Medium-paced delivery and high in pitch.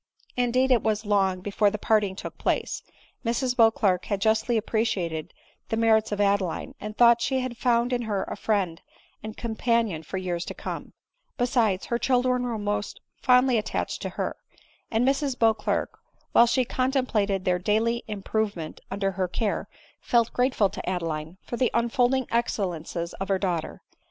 Yes: average, 160 wpm; high, 220 Hz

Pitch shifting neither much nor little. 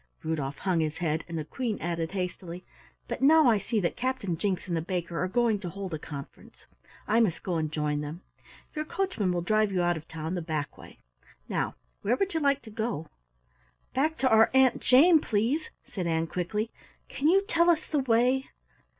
No: wide, 7.5 semitones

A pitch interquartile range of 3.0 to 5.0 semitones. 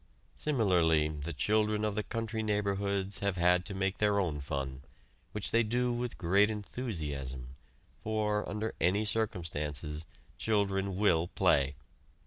Yes: average, 4.7 semitones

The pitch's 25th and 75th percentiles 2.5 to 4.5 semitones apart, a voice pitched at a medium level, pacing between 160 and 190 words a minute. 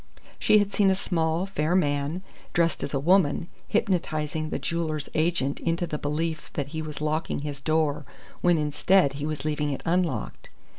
Yes: average, 2.8 semitones; medium, 155 Hz; average, 170 wpm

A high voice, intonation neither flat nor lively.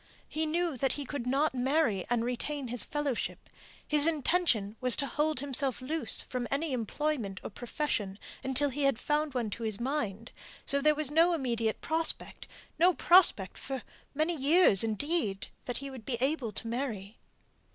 Yes: very high, 270 Hz; average, 4.5 semitones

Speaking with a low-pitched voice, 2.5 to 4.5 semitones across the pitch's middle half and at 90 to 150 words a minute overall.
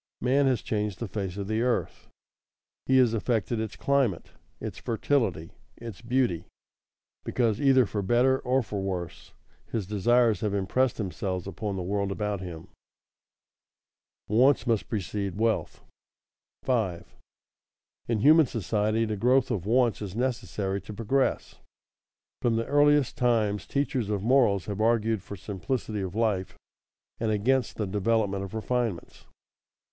Yes: low, 110 Hz; average, 3.6 semitones; average, 140 wpm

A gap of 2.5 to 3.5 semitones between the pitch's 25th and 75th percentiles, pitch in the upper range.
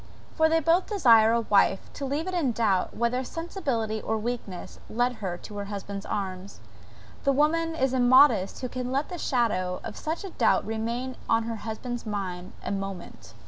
No: average, 5.3 semitones; high, 235 Hz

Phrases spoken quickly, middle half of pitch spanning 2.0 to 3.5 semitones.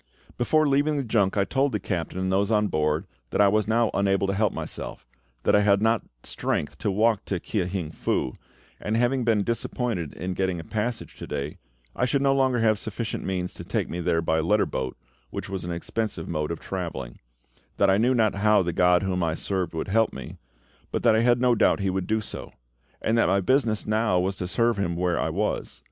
No: fast, 225 wpm; average, 4.0 semitones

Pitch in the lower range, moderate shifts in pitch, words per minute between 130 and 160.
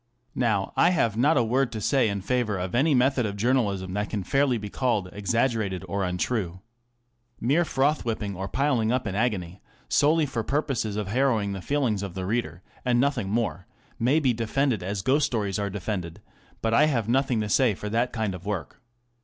No: low, 115 Hz; average, 4.6 semitones; average, 195 wpm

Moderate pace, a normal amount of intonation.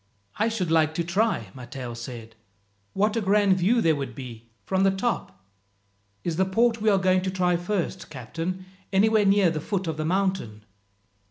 Yes: average, 180 wpm; average, 4.7 semitones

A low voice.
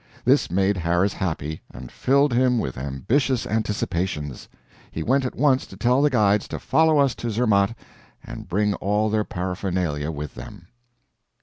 Yes: low, 100 Hz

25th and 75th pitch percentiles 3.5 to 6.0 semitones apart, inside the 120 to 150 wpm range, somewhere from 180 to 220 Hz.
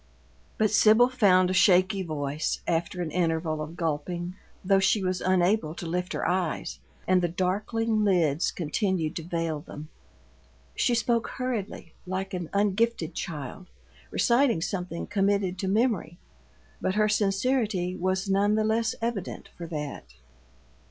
Yes: average, 3.8 semitones; average, 140 wpm; medium, 185 Hz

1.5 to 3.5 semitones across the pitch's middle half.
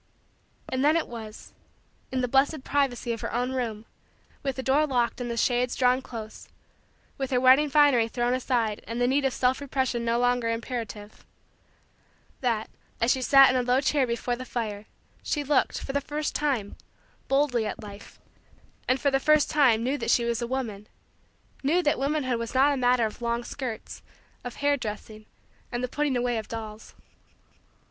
Yes: narrow, 2.6 semitones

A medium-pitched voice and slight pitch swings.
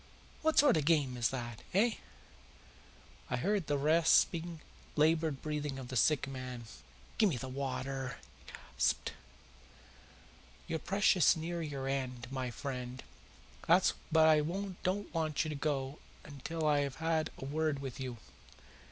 No: medium, 150 Hz; average, 3.7 semitones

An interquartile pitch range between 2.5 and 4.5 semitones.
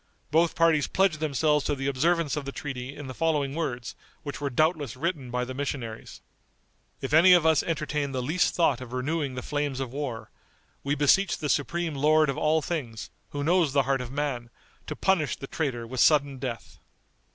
Yes: average, 3.2 semitones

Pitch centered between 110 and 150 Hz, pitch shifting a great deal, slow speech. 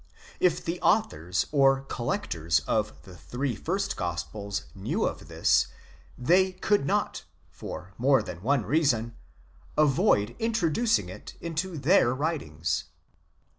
Yes: low, 135 Hz; wide, 8.8 semitones; slow, 120 wpm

